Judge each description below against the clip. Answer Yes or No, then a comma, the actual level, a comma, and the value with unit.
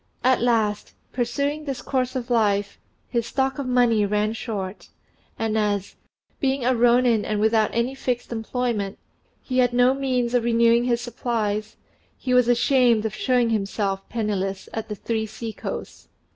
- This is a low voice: No, high, 235 Hz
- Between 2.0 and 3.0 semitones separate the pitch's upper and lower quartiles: Yes, average, 2.7 semitones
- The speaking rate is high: No, average, 160 wpm